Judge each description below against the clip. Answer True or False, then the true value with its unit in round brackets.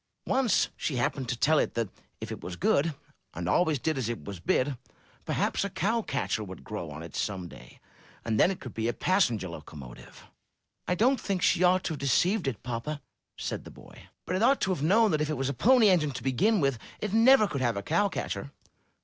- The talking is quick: True (225 wpm)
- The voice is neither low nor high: True (145 Hz)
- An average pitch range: False (8.5 semitones)